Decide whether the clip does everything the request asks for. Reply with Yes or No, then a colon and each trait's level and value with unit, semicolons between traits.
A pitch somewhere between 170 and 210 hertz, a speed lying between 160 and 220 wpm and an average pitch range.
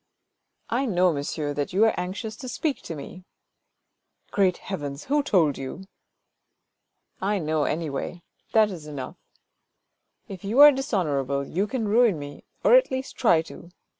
No: medium, 185 Hz; average, 170 wpm; wide, 6.9 semitones